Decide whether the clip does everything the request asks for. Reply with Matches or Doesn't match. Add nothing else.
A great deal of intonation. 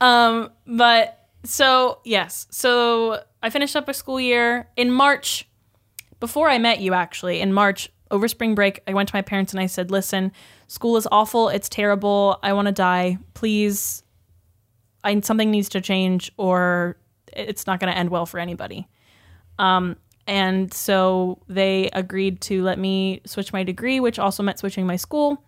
Doesn't match